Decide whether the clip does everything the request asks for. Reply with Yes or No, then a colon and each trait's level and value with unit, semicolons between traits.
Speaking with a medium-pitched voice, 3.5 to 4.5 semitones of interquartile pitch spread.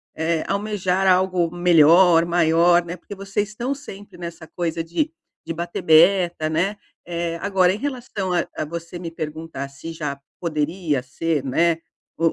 No: medium, 170 Hz; narrow, 2.6 semitones